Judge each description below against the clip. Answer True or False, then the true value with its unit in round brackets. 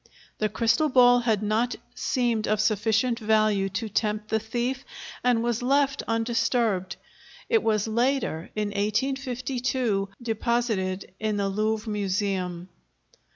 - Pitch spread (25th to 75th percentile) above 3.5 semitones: False (2.7 semitones)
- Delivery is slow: True (120 wpm)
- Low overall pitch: False (220 Hz)